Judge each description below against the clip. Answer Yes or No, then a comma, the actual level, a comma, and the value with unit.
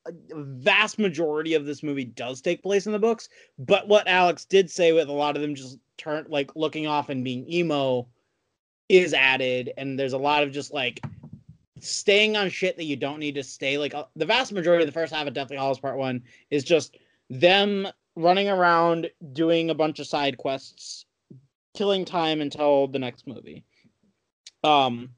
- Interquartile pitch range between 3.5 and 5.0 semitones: Yes, average, 4.2 semitones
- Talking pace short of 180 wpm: No, average, 190 wpm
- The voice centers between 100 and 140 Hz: No, medium, 150 Hz